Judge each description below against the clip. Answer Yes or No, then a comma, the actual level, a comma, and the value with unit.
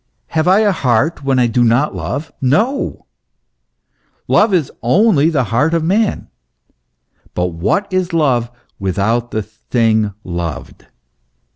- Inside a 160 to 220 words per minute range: No, average, 140 wpm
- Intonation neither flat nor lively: No, wide, 7.3 semitones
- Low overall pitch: Yes, low, 130 Hz